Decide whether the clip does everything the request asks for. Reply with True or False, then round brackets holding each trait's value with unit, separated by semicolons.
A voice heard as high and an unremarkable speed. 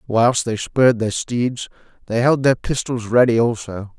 False (120 Hz; 165 wpm)